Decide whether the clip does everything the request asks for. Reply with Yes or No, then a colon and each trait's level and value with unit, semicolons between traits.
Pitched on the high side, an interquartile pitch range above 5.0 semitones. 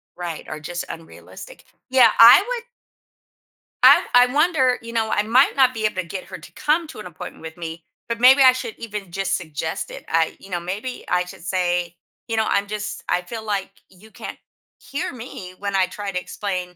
Yes: high, 205 Hz; wide, 5.6 semitones